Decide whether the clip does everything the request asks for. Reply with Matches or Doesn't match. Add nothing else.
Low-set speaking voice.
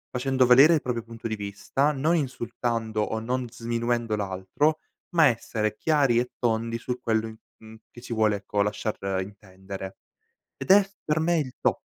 Matches